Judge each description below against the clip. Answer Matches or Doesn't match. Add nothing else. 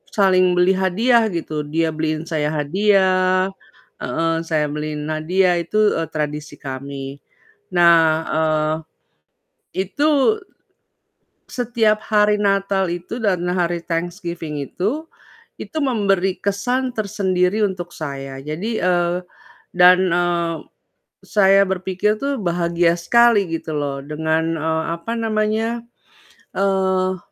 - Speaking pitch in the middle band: Matches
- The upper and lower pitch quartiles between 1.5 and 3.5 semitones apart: Doesn't match